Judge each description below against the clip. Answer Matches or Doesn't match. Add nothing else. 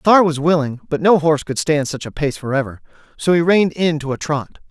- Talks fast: Matches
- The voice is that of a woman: Doesn't match